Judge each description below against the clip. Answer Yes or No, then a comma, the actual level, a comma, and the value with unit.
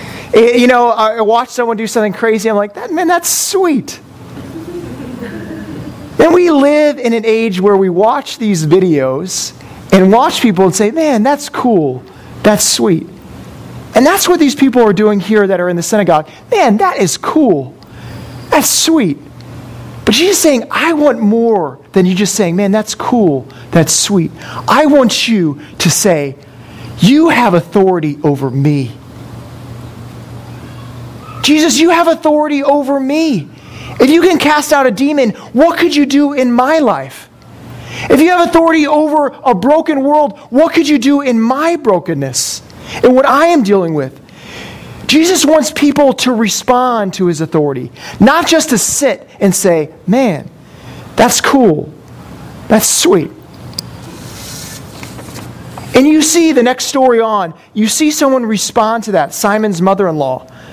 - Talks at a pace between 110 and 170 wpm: Yes, average, 150 wpm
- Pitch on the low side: No, high, 225 Hz